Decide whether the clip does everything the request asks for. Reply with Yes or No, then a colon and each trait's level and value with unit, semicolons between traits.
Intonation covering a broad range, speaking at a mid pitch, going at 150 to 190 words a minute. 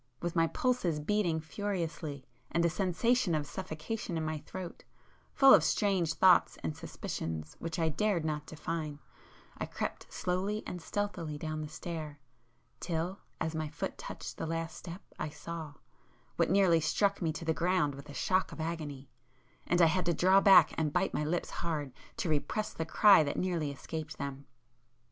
No: average, 3.3 semitones; medium, 165 Hz; average, 165 wpm